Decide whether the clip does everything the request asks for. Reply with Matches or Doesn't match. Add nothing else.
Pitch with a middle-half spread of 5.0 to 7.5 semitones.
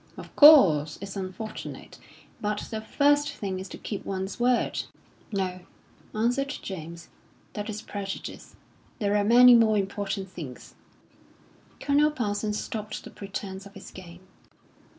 Doesn't match